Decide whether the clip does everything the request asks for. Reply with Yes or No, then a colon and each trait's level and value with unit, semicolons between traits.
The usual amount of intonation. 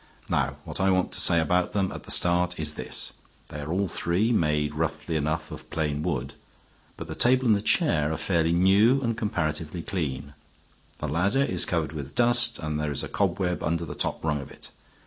Yes: average, 4.1 semitones